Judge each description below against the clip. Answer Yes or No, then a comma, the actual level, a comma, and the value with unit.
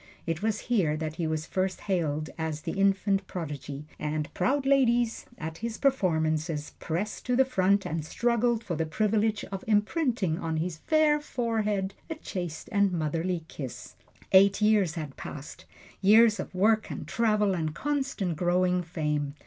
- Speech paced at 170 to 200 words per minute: No, average, 155 wpm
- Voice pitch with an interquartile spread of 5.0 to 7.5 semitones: Yes, wide, 5.6 semitones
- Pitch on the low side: No, high, 190 Hz